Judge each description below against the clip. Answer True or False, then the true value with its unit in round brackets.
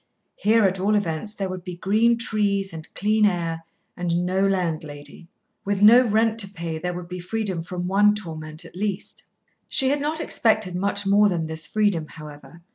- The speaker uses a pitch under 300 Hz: True (190 Hz)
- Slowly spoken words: False (185 wpm)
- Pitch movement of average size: True (3.7 semitones)